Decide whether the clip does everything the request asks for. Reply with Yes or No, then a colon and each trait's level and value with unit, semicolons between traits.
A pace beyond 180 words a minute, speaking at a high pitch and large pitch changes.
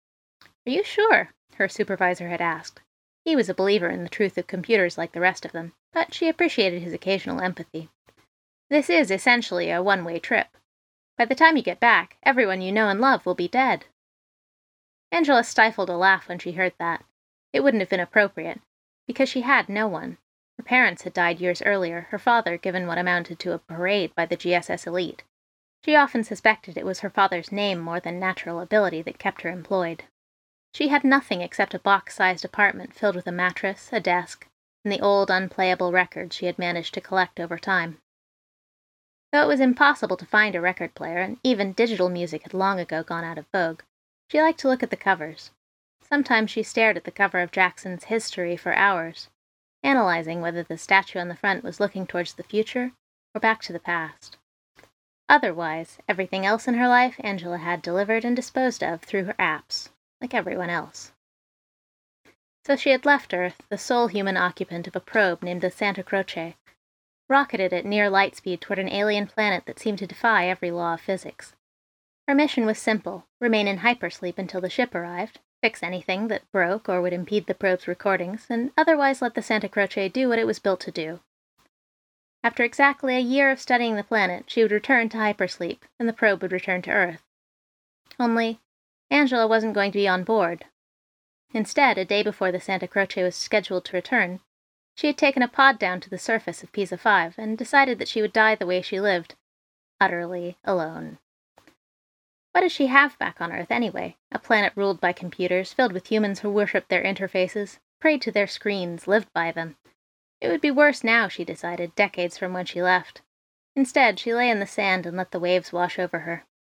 No: average, 195 wpm; high, 195 Hz; average, 4.2 semitones